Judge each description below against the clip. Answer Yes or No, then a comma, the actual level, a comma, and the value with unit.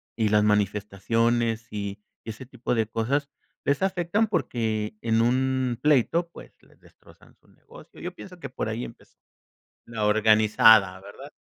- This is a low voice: Yes, low, 115 Hz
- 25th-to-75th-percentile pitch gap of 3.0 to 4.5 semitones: Yes, average, 3.7 semitones